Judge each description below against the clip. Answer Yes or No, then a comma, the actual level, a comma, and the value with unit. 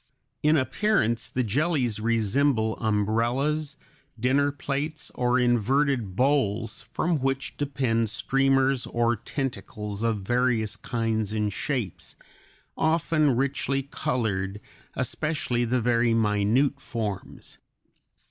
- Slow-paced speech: Yes, slow, 100 wpm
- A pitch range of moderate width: Yes, average, 4.0 semitones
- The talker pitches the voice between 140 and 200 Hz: No, low, 125 Hz